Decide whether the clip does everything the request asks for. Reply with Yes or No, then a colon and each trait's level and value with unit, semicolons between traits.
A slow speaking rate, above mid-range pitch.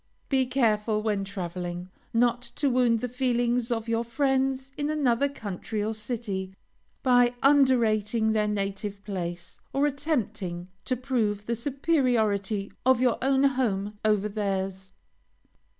Yes: slow, 130 wpm; high, 230 Hz